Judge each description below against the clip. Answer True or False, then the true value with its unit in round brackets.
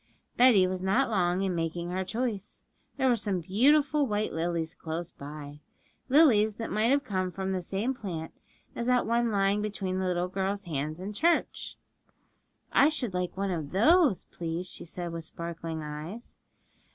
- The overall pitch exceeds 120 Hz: True (190 Hz)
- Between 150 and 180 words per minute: True (170 wpm)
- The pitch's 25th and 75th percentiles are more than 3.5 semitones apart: True (4.8 semitones)